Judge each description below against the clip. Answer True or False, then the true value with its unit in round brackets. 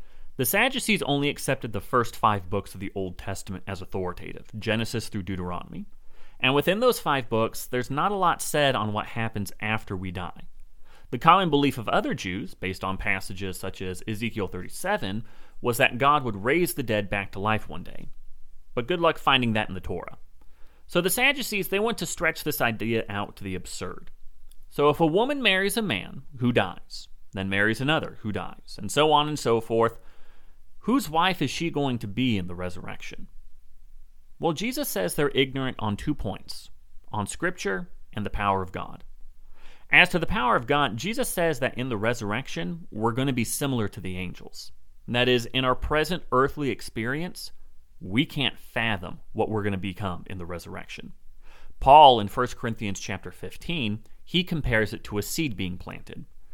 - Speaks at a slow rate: False (190 wpm)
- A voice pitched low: True (110 Hz)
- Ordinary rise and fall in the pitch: False (7.3 semitones)